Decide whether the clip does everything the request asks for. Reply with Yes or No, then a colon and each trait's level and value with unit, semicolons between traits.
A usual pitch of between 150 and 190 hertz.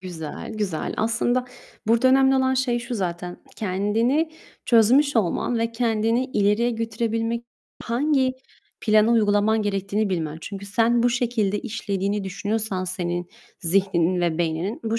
No: high, 215 Hz